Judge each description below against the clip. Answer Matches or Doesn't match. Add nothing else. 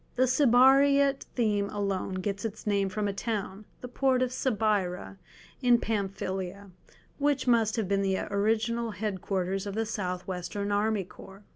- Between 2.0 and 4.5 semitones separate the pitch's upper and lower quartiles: Matches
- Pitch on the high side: Matches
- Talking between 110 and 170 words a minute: Matches